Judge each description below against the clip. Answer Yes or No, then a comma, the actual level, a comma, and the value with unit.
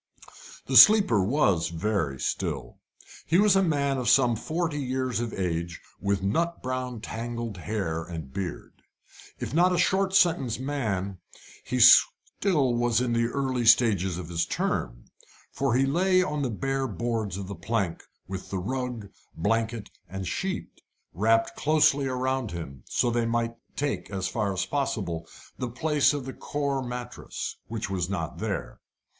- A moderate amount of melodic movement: No, wide, 6.1 semitones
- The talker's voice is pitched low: Yes, low, 120 Hz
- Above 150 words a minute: Yes, average, 160 wpm